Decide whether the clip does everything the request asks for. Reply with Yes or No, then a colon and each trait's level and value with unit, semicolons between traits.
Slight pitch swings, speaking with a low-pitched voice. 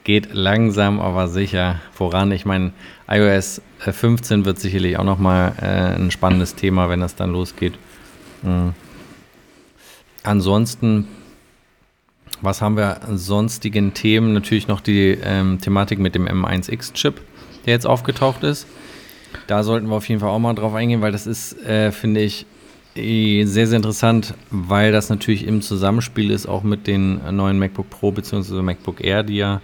Yes: narrow, 2.3 semitones; low, 100 Hz